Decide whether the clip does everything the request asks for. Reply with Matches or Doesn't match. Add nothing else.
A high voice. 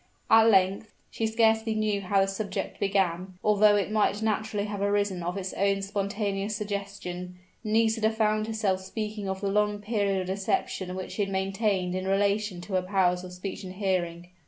Matches